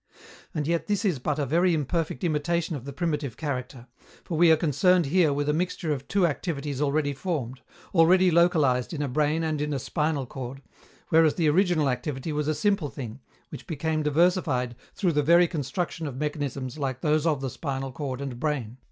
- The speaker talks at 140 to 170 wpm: No, average, 195 wpm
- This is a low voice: No, medium, 150 Hz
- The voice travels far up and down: No, average, 3.4 semitones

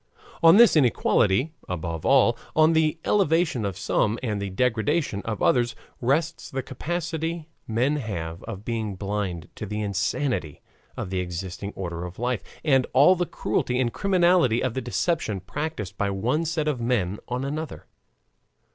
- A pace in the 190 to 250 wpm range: No, average, 155 wpm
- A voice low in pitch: Yes, low, 120 Hz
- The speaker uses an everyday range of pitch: No, wide, 7.5 semitones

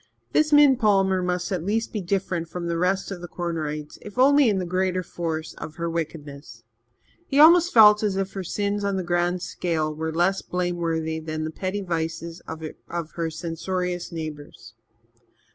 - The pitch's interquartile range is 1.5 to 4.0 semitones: Yes, average, 3.2 semitones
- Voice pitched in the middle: Yes, medium, 175 Hz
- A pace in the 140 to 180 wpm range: Yes, average, 175 wpm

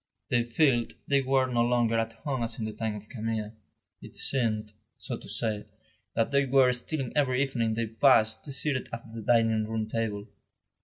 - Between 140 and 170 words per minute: No, average, 185 wpm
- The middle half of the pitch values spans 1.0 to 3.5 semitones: Yes, average, 2.7 semitones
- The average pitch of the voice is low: Yes, low, 115 Hz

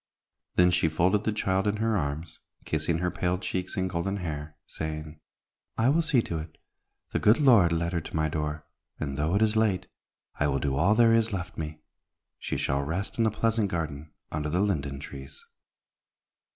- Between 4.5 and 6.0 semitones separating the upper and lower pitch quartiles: Yes, average, 5.1 semitones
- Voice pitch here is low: Yes, very low, 85 Hz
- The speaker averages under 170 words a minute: No, average, 190 wpm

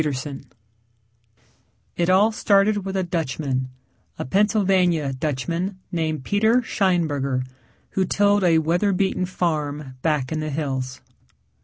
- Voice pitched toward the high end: No, medium, 170 Hz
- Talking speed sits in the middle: No, slow, 120 wpm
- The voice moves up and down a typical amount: Yes, average, 5.0 semitones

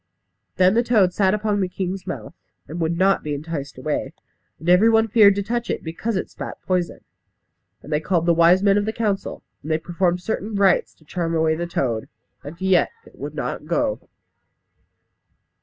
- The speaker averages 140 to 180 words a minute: No, average, 190 wpm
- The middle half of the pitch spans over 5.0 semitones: No, average, 3.6 semitones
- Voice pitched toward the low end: No, medium, 180 Hz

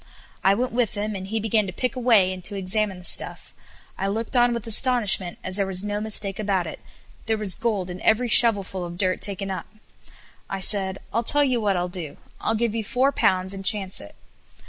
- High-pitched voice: Yes, high, 205 Hz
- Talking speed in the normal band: No, fast, 225 wpm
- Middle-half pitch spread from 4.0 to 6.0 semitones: No, average, 3.1 semitones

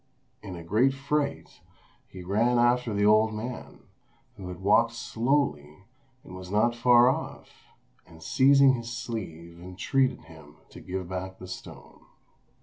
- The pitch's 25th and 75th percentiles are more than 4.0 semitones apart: Yes, average, 4.9 semitones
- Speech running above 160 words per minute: No, average, 145 wpm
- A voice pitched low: Yes, low, 110 Hz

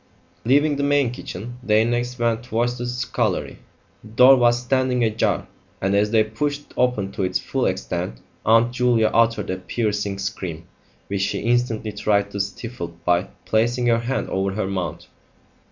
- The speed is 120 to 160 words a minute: No, average, 170 wpm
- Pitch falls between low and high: No, low, 115 Hz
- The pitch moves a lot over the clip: No, average, 3.4 semitones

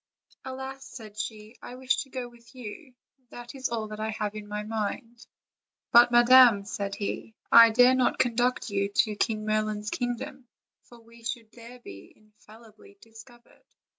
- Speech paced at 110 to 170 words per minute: Yes, average, 165 wpm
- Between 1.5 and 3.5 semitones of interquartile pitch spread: Yes, narrow, 2.4 semitones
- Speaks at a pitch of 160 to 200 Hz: No, high, 230 Hz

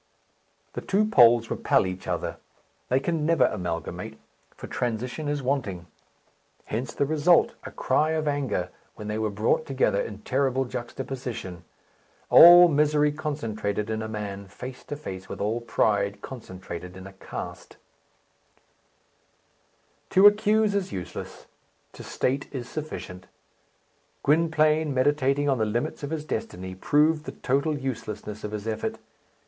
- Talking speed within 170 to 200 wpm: No, average, 140 wpm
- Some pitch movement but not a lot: No, wide, 6.1 semitones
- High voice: No, low, 125 Hz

